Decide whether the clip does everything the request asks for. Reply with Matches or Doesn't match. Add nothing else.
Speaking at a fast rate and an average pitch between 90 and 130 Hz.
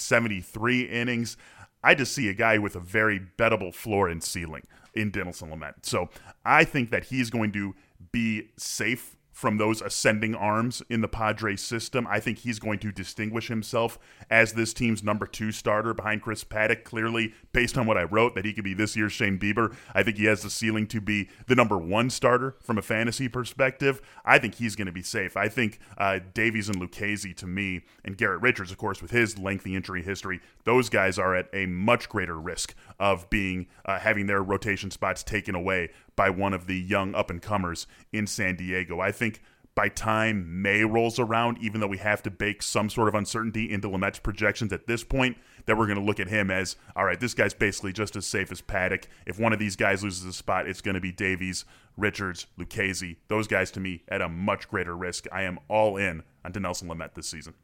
Matches